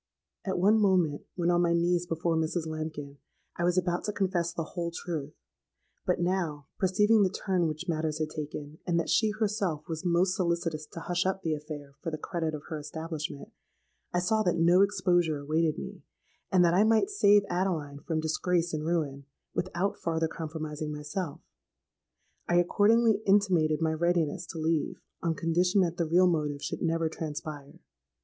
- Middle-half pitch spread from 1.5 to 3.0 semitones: Yes, average, 2.7 semitones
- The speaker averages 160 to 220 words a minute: Yes, average, 175 wpm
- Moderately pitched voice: Yes, medium, 170 Hz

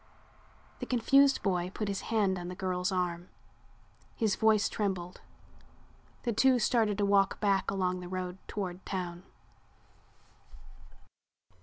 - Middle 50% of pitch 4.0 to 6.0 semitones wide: No, average, 2.9 semitones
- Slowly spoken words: Yes, slow, 125 wpm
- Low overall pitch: No, high, 195 Hz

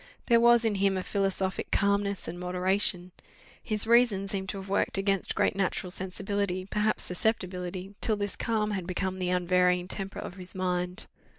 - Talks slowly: No, average, 170 wpm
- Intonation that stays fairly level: Yes, narrow, 1.9 semitones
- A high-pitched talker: Yes, high, 195 Hz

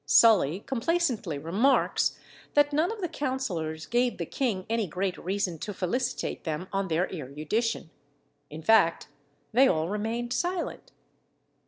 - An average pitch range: No, wide, 7.3 semitones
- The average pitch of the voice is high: Yes, high, 205 Hz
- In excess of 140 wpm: No, slow, 135 wpm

